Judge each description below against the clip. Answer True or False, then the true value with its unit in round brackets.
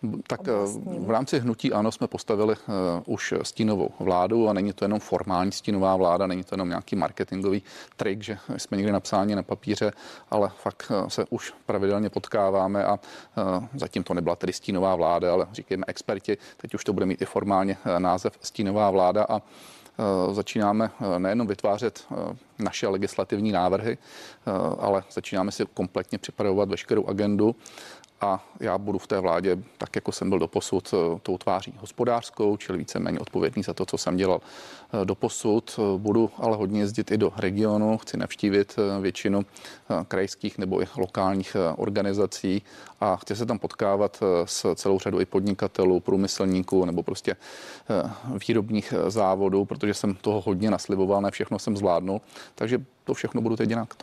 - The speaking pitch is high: False (100 Hz)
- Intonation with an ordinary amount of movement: False (1.9 semitones)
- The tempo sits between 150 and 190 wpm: True (155 wpm)